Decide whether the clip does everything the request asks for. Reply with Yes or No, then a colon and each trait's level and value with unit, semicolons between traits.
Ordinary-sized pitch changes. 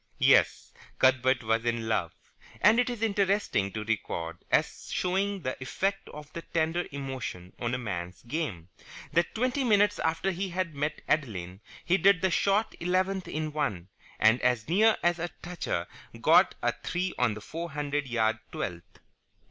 No: wide, 8.7 semitones